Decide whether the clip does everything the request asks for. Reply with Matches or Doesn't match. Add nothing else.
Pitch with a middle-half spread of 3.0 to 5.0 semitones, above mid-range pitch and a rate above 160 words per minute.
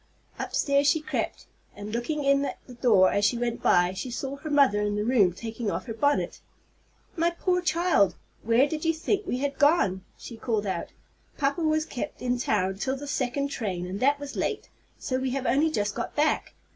Doesn't match